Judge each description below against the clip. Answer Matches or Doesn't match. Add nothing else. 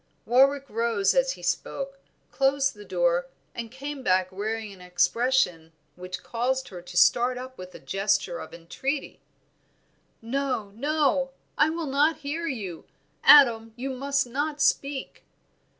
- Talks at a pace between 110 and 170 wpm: Matches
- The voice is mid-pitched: Doesn't match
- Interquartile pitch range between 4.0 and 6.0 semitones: Matches